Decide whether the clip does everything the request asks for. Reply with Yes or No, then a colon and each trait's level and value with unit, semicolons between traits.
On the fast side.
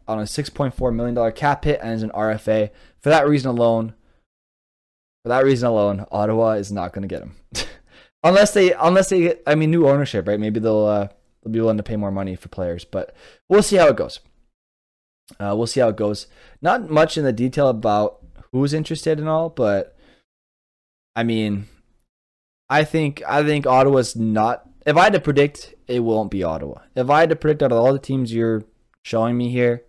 Yes: fast, 210 wpm